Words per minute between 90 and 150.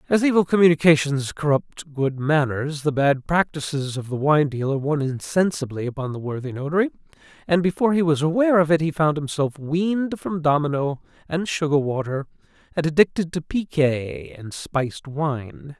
No: average, 160 wpm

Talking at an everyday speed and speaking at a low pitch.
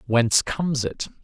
Yes: average, 145 wpm; low, 125 Hz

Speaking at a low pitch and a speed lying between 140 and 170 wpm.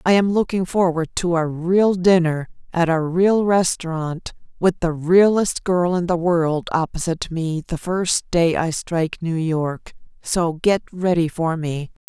No: medium, 170 Hz; average, 165 wpm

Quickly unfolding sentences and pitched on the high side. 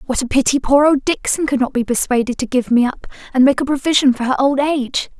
Yes: fast, 255 wpm; very high, 265 Hz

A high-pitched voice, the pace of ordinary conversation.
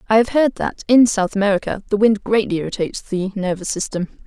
Yes: high, 205 Hz; average, 195 wpm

